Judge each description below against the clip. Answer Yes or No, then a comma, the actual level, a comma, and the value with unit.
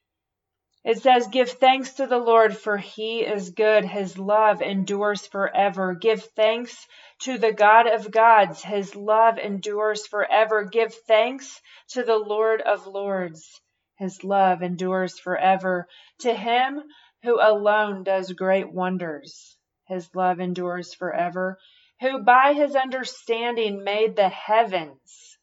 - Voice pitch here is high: Yes, high, 210 Hz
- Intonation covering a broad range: No, average, 3.5 semitones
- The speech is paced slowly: Yes, slow, 130 wpm